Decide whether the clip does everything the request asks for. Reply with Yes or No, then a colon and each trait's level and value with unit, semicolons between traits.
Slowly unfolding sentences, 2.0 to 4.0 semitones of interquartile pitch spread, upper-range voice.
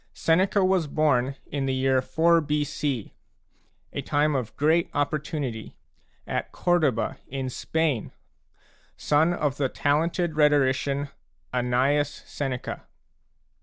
No: slow, 105 wpm; average, 2.9 semitones; medium, 145 Hz